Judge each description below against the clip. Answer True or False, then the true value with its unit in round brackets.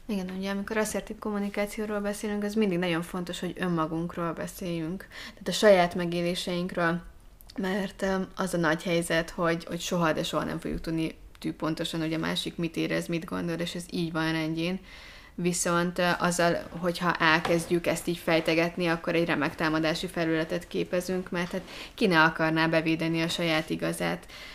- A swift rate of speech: True (160 wpm)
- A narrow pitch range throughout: True (2.3 semitones)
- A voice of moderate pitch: True (175 Hz)